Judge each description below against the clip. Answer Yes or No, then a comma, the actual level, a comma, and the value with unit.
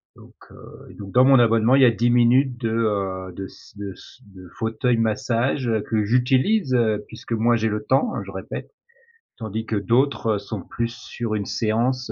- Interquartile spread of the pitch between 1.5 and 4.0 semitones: Yes, average, 2.7 semitones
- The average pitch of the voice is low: Yes, low, 115 Hz